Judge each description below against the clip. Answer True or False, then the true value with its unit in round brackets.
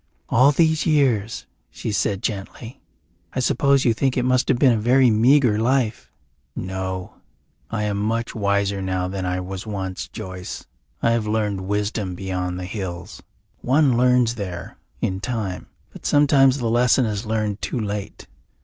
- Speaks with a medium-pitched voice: False (110 Hz)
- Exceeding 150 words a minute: True (160 wpm)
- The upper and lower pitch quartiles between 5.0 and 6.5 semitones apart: False (4.5 semitones)